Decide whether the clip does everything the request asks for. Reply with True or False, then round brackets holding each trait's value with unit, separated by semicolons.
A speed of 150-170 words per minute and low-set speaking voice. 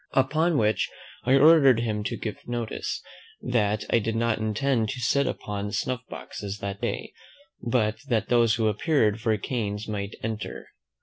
True (160 wpm; 115 Hz)